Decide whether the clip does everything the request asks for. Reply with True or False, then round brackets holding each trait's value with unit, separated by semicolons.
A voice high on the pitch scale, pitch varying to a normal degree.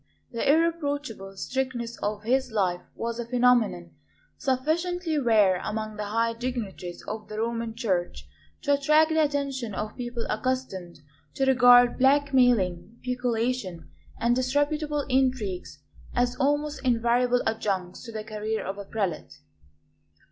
True (240 Hz; 3.9 semitones)